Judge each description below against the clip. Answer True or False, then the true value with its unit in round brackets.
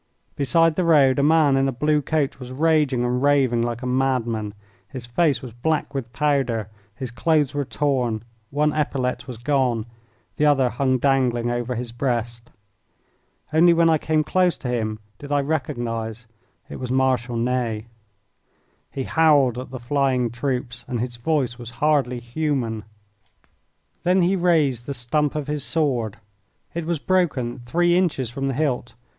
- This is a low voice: True (130 Hz)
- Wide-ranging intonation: False (3.8 semitones)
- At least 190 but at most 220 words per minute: False (165 wpm)